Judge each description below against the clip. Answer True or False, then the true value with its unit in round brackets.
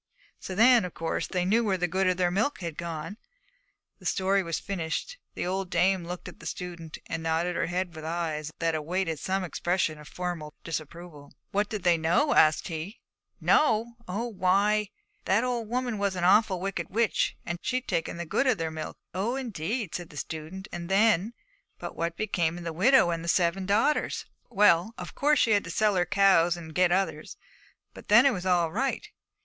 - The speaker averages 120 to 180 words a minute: False (200 wpm)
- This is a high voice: False (180 Hz)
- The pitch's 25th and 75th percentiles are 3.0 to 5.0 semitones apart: True (3.8 semitones)